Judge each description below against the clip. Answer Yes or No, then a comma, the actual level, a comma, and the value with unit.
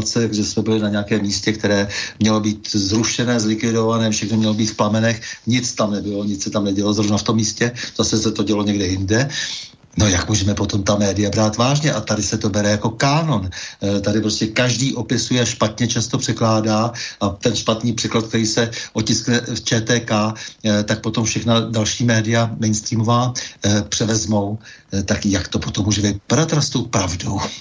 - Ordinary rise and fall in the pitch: No, narrow, 1.9 semitones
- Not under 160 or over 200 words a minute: Yes, fast, 170 wpm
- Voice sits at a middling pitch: No, low, 110 Hz